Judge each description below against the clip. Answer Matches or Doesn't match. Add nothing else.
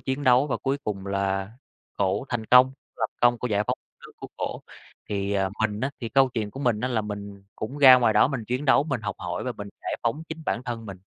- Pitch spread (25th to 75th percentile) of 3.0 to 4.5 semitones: Matches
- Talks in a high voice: Doesn't match